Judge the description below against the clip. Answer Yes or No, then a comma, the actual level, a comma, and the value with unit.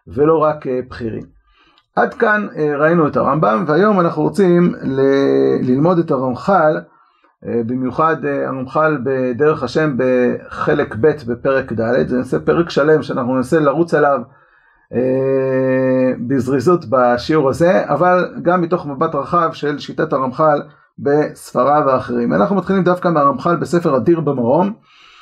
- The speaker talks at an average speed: Yes, average, 120 wpm